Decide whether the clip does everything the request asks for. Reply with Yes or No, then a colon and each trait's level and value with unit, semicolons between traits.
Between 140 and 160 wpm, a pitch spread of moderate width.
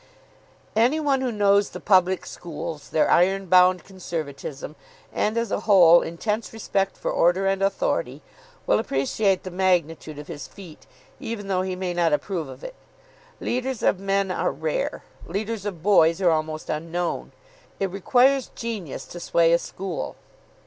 Yes: average, 155 wpm; average, 3.6 semitones